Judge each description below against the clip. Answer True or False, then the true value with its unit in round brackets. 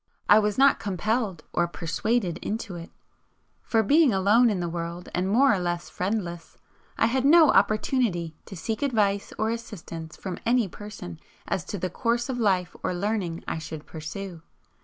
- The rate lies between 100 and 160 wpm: False (170 wpm)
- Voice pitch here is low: False (200 Hz)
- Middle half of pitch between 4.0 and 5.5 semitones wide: True (4.6 semitones)